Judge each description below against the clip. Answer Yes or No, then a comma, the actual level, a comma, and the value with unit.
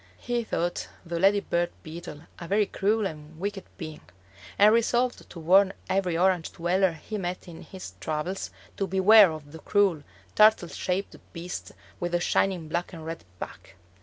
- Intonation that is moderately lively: Yes, average, 3.2 semitones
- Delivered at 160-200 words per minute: Yes, average, 165 wpm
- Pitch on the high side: No, medium, 180 Hz